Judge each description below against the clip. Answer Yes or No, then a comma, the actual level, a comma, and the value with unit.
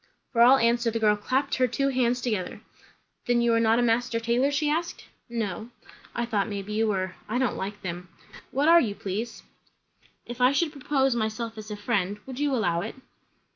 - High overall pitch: Yes, high, 235 Hz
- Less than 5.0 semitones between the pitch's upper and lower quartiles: Yes, average, 3.4 semitones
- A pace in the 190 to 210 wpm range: Yes, average, 200 wpm